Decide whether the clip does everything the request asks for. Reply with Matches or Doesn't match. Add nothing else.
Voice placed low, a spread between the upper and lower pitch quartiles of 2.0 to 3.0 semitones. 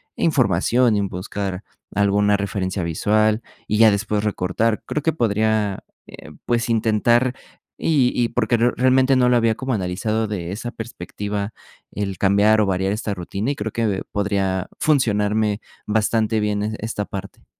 Matches